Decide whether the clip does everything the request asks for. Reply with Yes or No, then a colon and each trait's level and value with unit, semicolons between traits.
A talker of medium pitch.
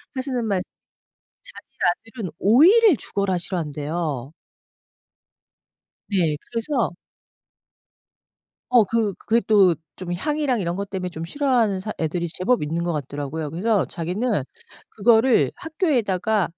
No: high, 200 Hz